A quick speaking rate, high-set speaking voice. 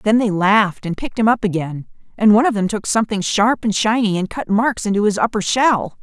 Yes: fast, 240 wpm; high, 210 Hz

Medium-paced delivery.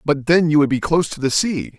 No: fast, 300 wpm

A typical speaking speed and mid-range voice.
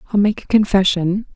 No: average, 180 wpm; high, 200 Hz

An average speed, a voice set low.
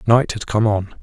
No: fast, 235 wpm; low, 110 Hz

